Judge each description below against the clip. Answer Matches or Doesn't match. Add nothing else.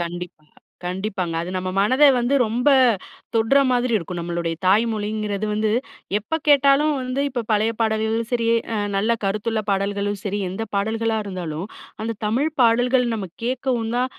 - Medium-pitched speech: Doesn't match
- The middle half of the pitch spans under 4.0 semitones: Matches